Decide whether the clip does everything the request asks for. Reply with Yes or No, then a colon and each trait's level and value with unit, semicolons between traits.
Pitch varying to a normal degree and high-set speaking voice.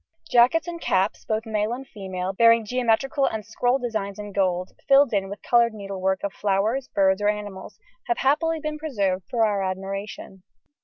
Yes: average, 4.2 semitones; high, 210 Hz